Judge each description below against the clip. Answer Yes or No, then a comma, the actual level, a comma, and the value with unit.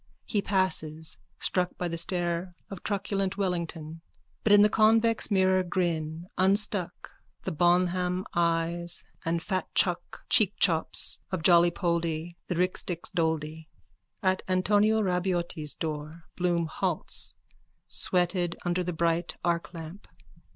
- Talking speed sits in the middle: No, slow, 110 wpm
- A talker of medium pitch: Yes, medium, 175 Hz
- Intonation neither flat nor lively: No, narrow, 2.0 semitones